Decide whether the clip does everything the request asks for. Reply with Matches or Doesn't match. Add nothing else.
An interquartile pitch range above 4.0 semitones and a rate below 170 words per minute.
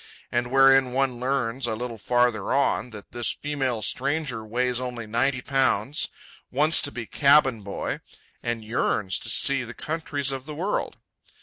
Doesn't match